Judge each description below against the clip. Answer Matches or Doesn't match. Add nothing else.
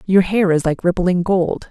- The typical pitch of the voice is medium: Matches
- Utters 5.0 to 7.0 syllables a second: Doesn't match